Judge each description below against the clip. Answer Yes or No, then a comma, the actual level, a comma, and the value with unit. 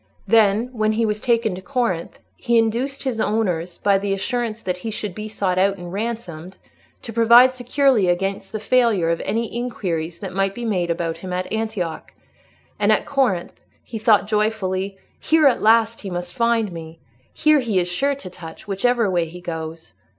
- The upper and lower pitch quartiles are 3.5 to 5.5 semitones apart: Yes, average, 4.4 semitones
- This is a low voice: No, high, 210 Hz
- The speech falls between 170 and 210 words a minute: Yes, average, 185 wpm